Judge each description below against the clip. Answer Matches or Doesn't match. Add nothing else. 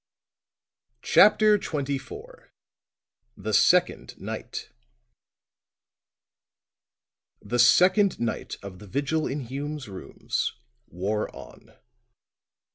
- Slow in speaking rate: Matches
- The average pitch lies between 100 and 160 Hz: Matches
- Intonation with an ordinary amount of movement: Doesn't match